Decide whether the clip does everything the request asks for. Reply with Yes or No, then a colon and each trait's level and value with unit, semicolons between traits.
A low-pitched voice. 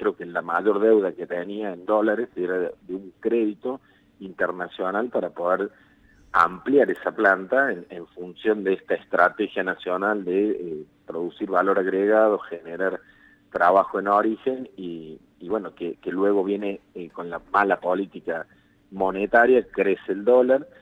Yes: low, 100 Hz